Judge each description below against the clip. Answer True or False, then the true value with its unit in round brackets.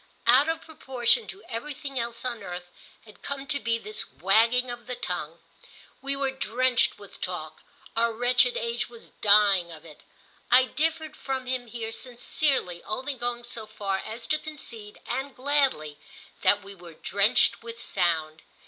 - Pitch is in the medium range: False (235 Hz)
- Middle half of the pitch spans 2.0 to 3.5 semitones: False (4.6 semitones)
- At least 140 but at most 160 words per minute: True (155 wpm)